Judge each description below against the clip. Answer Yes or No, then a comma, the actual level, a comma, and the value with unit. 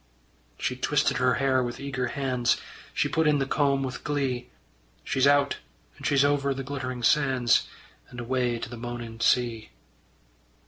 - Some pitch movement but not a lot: No, narrow, 2.3 semitones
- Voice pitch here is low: Yes, low, 130 Hz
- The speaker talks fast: No, average, 155 wpm